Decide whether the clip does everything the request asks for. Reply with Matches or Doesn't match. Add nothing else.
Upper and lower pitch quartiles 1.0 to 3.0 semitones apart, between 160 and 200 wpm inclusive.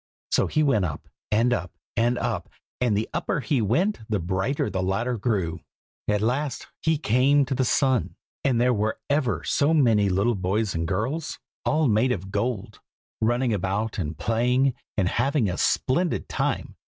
Doesn't match